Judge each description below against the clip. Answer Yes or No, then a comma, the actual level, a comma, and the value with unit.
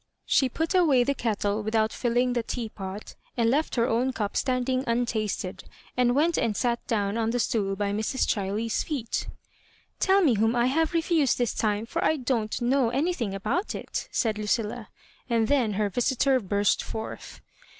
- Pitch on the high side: Yes, high, 235 Hz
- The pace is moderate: Yes, average, 180 wpm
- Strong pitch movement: No, average, 3.4 semitones